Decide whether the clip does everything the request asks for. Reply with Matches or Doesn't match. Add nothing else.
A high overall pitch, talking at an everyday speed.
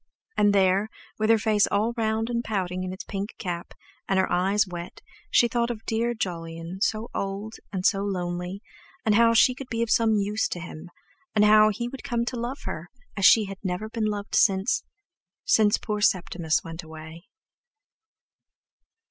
Matches